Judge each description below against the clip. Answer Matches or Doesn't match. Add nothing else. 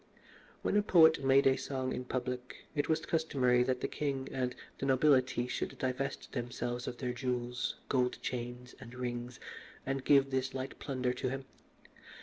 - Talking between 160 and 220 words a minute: Matches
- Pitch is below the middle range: Matches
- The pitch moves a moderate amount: Doesn't match